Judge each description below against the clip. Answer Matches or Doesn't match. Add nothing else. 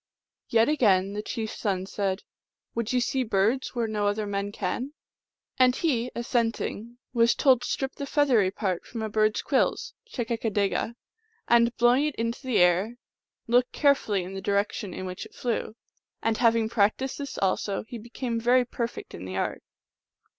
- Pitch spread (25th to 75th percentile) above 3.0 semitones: Matches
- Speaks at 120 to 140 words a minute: Doesn't match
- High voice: Matches